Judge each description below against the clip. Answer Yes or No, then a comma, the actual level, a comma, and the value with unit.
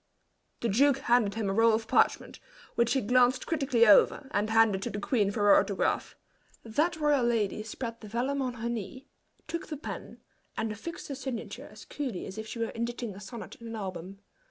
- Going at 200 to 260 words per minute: Yes, fast, 205 wpm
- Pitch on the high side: Yes, high, 230 Hz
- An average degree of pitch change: Yes, average, 3.6 semitones